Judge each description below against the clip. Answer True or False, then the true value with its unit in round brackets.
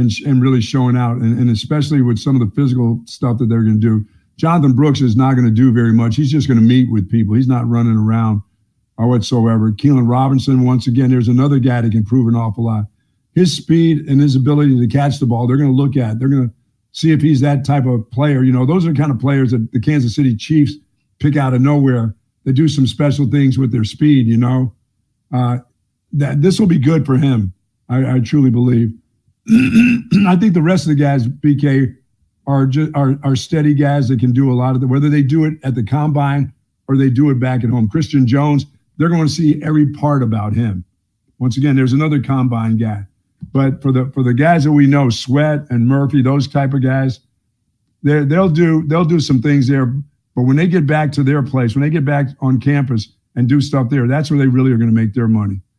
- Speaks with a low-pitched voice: True (130 Hz)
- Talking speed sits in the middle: False (235 wpm)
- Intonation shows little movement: False (3.3 semitones)